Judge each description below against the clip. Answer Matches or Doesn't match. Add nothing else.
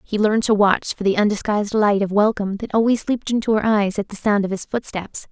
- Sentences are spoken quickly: Matches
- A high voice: Matches